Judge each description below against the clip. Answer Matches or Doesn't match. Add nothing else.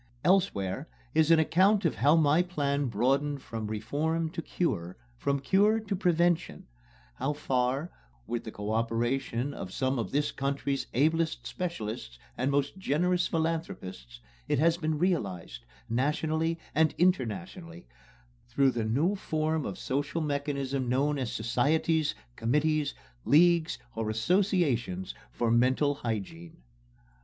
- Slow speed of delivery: Matches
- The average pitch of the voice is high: Doesn't match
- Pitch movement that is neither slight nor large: Doesn't match